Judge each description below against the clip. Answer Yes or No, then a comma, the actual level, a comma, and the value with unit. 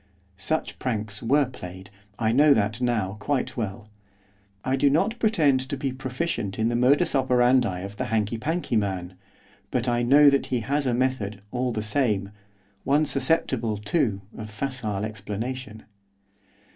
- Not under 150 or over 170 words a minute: Yes, average, 155 wpm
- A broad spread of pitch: No, average, 4.2 semitones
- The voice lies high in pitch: No, low, 120 Hz